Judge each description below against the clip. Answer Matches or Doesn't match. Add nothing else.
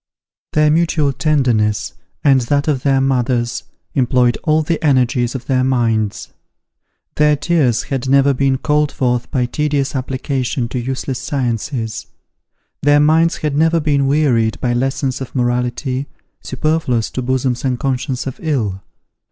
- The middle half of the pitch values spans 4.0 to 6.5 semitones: Doesn't match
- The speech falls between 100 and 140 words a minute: Matches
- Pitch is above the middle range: Doesn't match